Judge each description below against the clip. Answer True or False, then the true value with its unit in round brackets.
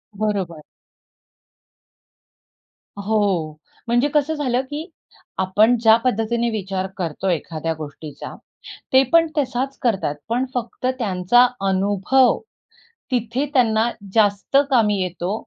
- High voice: True (220 Hz)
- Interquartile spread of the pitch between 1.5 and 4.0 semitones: False (4.9 semitones)